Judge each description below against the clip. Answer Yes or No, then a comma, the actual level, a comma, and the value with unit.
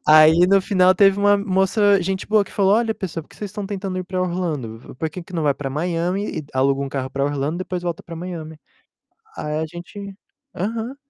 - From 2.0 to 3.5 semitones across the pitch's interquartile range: No, average, 4.1 semitones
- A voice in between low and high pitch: Yes, medium, 180 Hz